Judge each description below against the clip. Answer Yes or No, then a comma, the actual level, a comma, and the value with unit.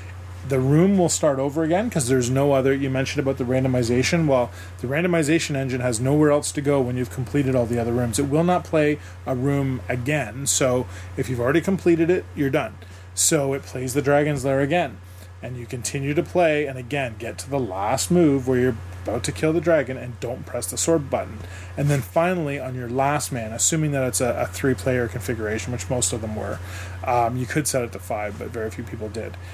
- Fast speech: Yes, fast, 225 wpm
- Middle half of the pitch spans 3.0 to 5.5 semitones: Yes, average, 3.8 semitones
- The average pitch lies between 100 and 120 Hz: No, low, 130 Hz